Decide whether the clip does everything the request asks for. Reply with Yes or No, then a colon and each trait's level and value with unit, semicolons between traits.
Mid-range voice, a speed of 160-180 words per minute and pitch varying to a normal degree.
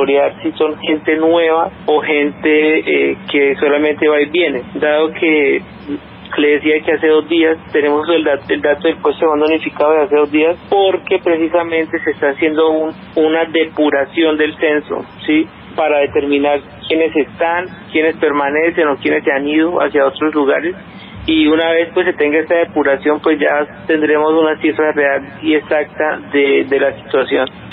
No: medium, 155 Hz; average, 170 wpm; narrow, 1.6 semitones